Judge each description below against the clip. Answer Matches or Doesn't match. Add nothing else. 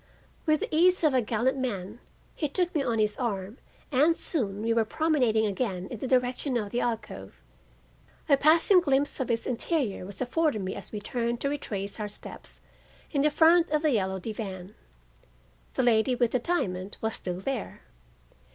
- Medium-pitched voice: Doesn't match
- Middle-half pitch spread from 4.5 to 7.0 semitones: Matches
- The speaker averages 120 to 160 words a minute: Doesn't match